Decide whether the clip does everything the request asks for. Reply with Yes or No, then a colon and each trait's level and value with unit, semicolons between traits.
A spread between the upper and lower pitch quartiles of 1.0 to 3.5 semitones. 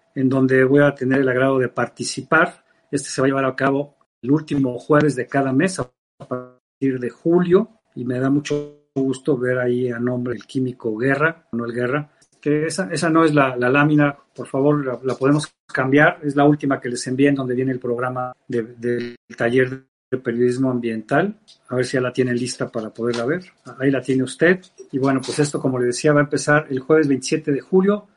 Yes: average, 2.8 semitones